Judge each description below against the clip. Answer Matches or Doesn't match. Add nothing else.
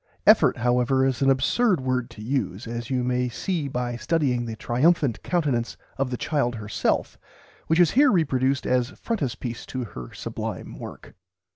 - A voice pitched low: Matches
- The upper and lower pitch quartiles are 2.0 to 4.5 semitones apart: Matches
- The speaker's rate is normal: Matches